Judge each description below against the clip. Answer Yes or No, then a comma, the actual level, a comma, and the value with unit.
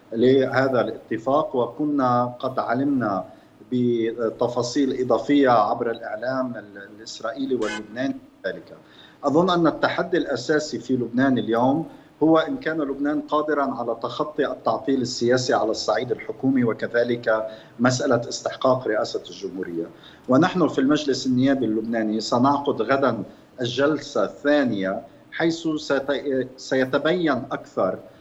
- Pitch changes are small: No, average, 3.3 semitones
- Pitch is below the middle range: Yes, low, 130 Hz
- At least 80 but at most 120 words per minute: Yes, average, 100 wpm